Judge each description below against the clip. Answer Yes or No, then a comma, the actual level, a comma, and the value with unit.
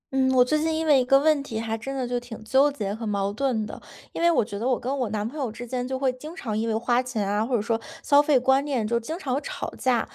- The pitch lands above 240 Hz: Yes, very high, 250 Hz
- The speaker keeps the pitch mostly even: No, average, 3.6 semitones